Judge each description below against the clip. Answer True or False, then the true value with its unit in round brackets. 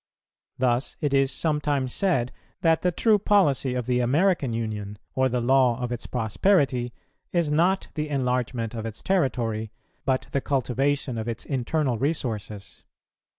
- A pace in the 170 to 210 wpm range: False (150 wpm)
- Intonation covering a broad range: False (4.0 semitones)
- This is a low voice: True (130 Hz)